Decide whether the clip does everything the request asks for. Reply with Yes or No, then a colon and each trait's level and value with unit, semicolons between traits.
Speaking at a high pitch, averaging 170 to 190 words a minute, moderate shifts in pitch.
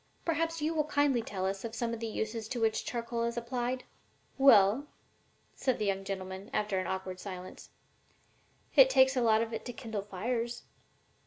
Yes: high, 230 Hz; average, 175 wpm; average, 4.1 semitones